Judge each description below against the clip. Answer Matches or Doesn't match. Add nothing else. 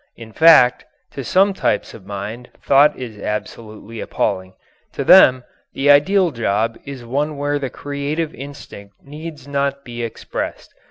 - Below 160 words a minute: Matches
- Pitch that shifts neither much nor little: Matches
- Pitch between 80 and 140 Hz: Matches